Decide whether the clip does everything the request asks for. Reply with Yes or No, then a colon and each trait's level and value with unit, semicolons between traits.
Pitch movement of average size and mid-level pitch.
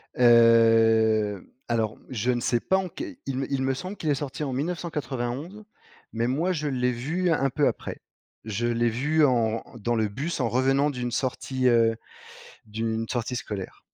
No: average, 4.1 semitones; low, 125 Hz